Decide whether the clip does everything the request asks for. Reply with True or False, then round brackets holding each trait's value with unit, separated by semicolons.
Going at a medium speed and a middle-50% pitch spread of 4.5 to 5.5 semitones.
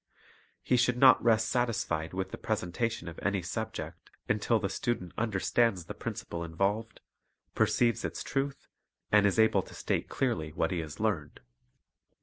True (150 wpm; 4.9 semitones)